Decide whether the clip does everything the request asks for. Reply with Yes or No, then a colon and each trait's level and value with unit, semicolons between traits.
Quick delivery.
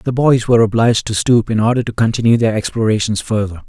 Yes: fast, 210 wpm